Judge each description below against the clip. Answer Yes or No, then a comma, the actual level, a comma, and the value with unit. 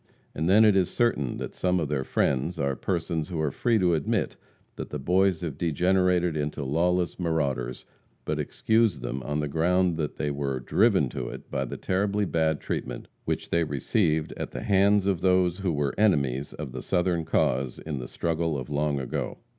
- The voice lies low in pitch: Yes, very low, 80 Hz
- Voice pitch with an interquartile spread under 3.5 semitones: No, average, 4.3 semitones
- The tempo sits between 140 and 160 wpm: No, average, 195 wpm